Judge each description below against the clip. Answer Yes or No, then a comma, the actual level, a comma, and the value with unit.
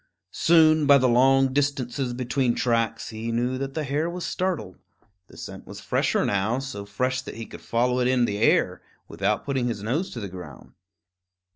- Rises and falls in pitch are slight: No, average, 3.1 semitones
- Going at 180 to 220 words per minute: Yes, average, 185 wpm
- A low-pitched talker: Yes, low, 125 Hz